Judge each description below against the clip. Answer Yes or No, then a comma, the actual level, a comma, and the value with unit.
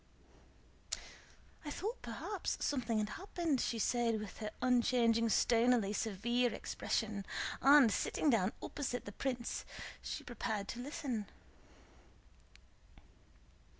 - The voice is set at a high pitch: Yes, high, 235 Hz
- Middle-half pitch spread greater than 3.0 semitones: No, average, 2.7 semitones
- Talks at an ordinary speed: No, slow, 110 wpm